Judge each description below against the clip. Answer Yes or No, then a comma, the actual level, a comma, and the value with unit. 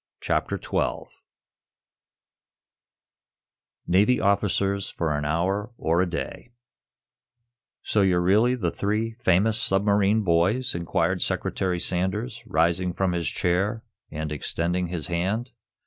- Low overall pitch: Yes, very low, 95 Hz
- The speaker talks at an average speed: No, slow, 110 wpm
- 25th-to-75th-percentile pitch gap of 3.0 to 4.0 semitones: Yes, average, 3.4 semitones